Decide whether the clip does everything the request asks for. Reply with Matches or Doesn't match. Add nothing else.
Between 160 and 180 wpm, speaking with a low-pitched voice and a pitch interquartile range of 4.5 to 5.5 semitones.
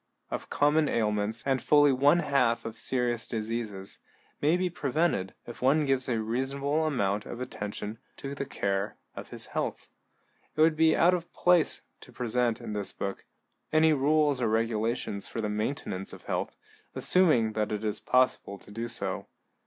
Matches